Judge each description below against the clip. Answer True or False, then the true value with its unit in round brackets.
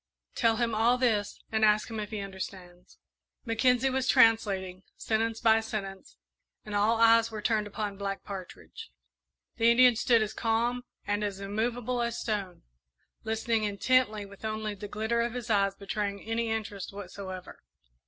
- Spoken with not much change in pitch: True (2.3 semitones)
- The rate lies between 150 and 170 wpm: True (155 wpm)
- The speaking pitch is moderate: False (220 Hz)